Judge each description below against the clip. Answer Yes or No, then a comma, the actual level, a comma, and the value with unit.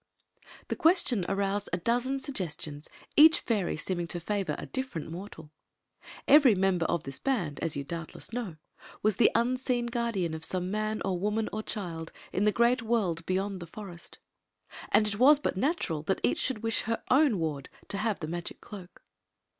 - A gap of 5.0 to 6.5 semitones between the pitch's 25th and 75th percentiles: Yes, wide, 5.5 semitones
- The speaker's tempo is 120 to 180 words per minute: Yes, average, 175 wpm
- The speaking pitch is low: No, high, 200 Hz